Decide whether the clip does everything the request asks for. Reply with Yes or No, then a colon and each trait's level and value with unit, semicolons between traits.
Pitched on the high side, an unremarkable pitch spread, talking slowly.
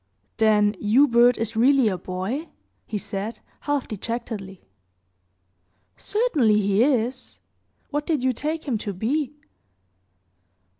Yes: high, 230 Hz; average, 5.0 semitones; slow, 110 wpm